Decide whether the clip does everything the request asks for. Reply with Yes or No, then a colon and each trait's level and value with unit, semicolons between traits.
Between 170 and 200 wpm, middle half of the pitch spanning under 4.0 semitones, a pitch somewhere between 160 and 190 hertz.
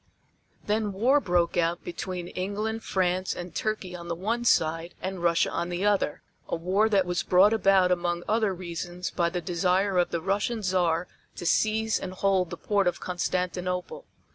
Yes: average, 175 wpm; narrow, 2.6 semitones; medium, 185 Hz